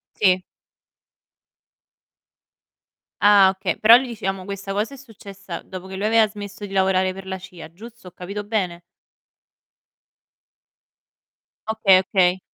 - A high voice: Yes, high, 195 Hz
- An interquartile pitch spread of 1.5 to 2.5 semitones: Yes, narrow, 2.1 semitones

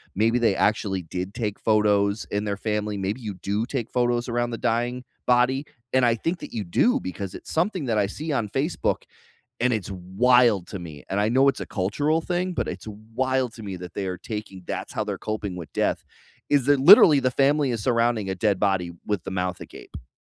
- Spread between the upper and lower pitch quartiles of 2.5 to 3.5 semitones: No, average, 4.3 semitones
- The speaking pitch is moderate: No, low, 110 Hz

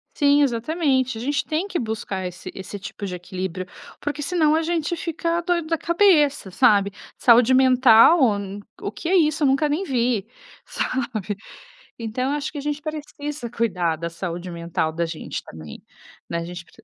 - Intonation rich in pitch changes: Yes, wide, 7.7 semitones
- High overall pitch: Yes, very high, 255 Hz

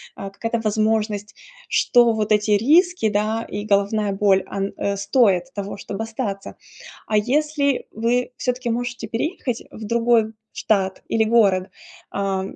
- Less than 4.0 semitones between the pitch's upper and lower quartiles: Yes, average, 2.9 semitones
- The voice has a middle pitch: No, high, 220 Hz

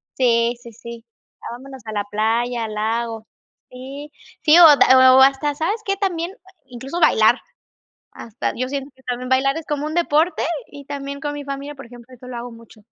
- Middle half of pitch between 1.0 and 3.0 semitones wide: No, average, 3.6 semitones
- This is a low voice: No, very high, 260 Hz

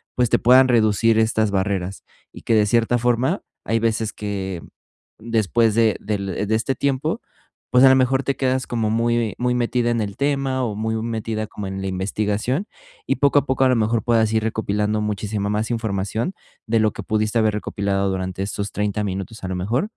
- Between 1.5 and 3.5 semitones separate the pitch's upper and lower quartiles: Yes, average, 2.7 semitones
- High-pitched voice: No, low, 110 Hz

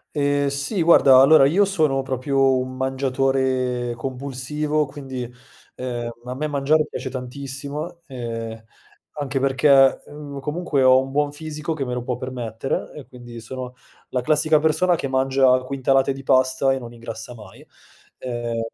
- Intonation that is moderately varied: No, narrow, 2.2 semitones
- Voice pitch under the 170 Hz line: Yes, low, 135 Hz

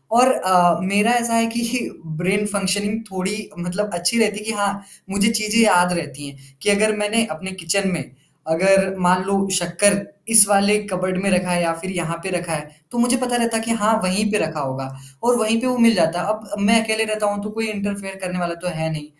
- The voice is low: No, high, 200 Hz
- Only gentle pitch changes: No, average, 3.4 semitones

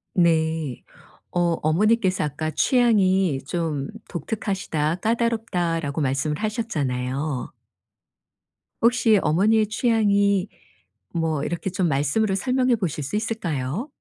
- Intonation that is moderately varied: No, wide, 6.2 semitones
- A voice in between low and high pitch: Yes, medium, 175 Hz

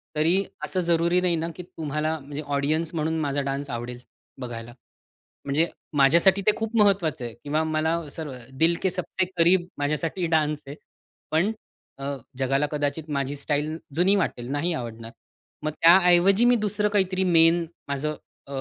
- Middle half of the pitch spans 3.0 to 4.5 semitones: Yes, average, 3.7 semitones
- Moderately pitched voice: Yes, medium, 155 Hz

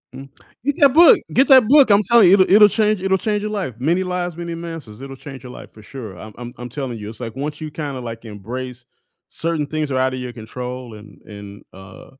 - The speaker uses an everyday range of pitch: No, wide, 7.7 semitones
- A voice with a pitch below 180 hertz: Yes, medium, 140 Hz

